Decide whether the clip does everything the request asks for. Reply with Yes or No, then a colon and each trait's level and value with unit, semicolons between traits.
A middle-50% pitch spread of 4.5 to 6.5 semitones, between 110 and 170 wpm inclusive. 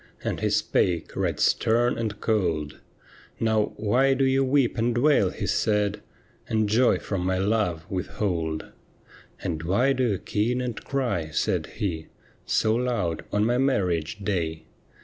Yes: average, 5.3 semitones; average, 160 wpm